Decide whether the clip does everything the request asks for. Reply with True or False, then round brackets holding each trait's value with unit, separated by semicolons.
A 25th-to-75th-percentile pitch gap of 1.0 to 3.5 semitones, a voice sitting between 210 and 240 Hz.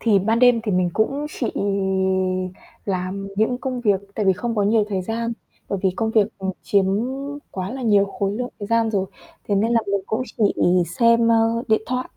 True (2.7 semitones; 220 Hz)